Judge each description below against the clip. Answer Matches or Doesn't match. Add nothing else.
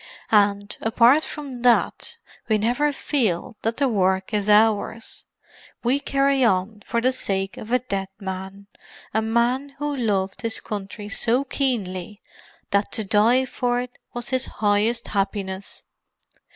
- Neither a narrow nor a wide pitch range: Matches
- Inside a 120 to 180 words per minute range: Matches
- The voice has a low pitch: Doesn't match